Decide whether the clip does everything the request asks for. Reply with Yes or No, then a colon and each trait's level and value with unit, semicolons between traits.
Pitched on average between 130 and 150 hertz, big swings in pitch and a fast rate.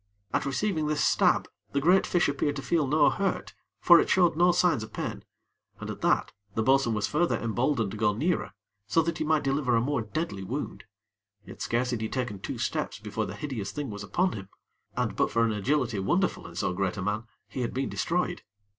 Yes: low, 135 Hz; wide, 6.3 semitones; fast, 215 wpm